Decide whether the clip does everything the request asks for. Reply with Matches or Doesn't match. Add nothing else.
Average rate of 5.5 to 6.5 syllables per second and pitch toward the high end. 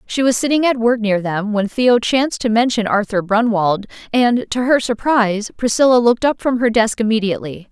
Matches